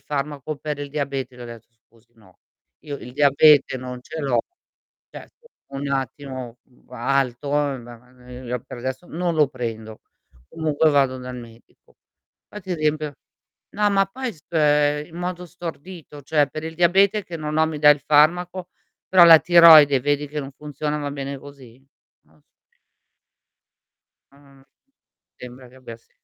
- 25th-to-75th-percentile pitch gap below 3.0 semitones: No, average, 3.6 semitones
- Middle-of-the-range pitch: Yes, medium, 145 Hz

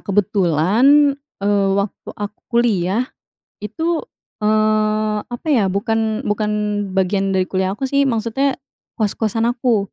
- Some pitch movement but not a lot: Yes, average, 3.3 semitones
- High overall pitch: Yes, high, 215 Hz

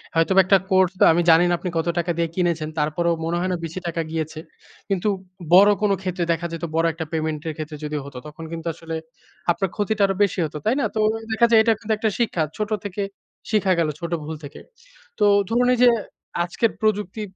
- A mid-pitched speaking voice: Yes, medium, 175 Hz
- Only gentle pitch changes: No, average, 4.1 semitones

